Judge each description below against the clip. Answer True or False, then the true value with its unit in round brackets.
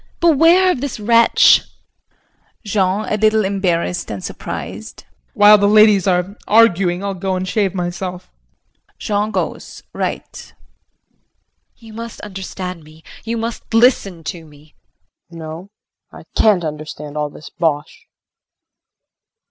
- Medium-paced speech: False (125 wpm)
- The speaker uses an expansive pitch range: False (3.9 semitones)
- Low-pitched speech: False (195 Hz)